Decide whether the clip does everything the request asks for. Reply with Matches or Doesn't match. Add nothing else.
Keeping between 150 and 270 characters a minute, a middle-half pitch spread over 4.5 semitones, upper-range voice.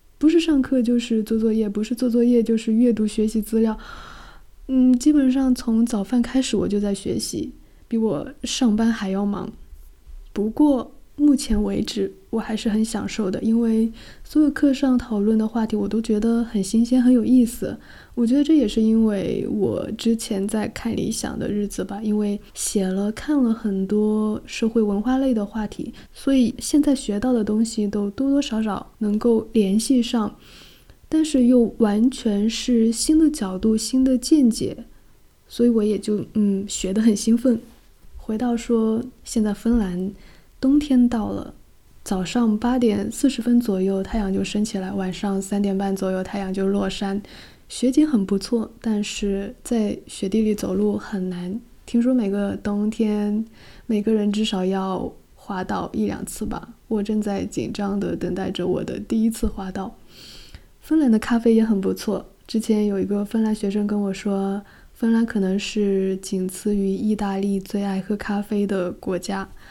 Doesn't match